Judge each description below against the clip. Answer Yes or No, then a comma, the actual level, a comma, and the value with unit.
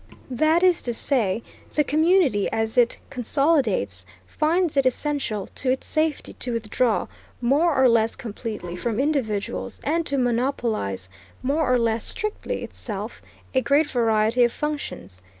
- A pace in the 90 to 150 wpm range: Yes, average, 140 wpm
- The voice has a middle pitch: No, very high, 250 Hz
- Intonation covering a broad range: No, average, 5.0 semitones